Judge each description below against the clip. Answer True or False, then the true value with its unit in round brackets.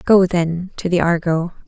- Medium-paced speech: True (180 wpm)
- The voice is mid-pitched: True (175 Hz)